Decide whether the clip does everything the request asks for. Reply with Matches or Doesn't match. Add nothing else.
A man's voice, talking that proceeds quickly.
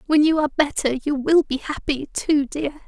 Doesn't match